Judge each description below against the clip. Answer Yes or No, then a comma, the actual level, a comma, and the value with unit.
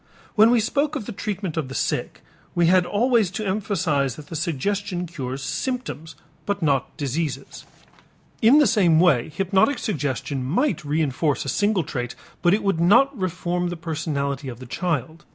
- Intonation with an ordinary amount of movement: No, wide, 5.9 semitones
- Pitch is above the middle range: No, medium, 175 Hz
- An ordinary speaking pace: Yes, average, 165 wpm